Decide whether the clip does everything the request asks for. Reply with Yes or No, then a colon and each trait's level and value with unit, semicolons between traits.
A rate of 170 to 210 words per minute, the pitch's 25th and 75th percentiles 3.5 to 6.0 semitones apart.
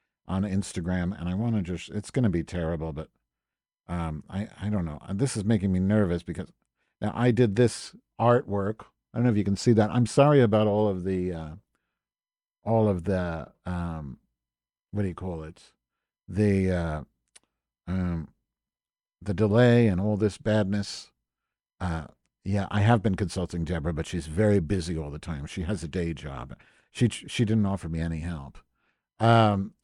Yes: average, 180 wpm; average, 4.3 semitones